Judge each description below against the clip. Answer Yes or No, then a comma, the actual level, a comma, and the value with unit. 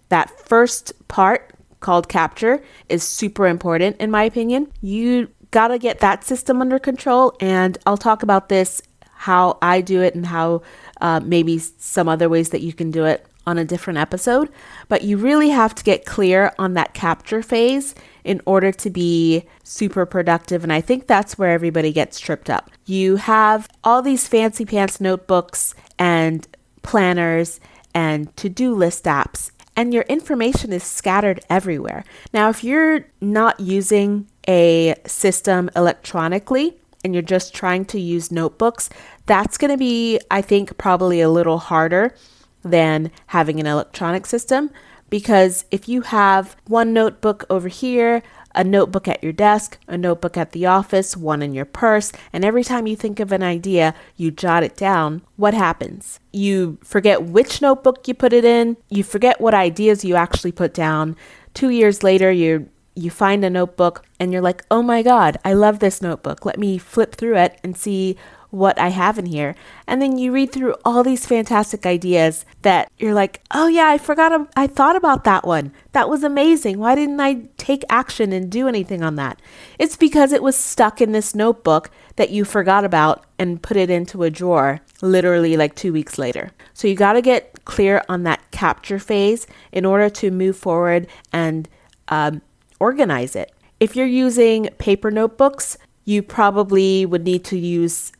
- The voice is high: Yes, high, 195 Hz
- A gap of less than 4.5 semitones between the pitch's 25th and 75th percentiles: No, average, 4.8 semitones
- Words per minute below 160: No, average, 175 wpm